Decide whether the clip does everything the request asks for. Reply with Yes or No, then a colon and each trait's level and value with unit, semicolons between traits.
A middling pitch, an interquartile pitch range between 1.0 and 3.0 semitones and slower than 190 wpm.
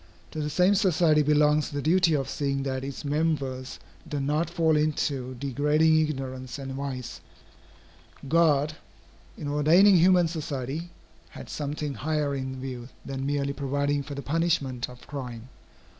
Yes: medium, 145 Hz; narrow, 2.6 semitones; average, 145 wpm